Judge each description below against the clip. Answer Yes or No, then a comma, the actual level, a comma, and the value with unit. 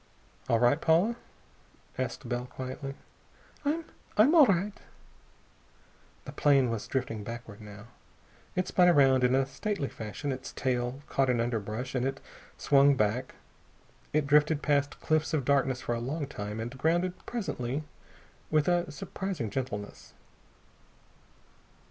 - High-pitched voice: No, low, 135 Hz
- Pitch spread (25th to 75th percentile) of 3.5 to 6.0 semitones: Yes, average, 4.3 semitones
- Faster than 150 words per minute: No, slow, 135 wpm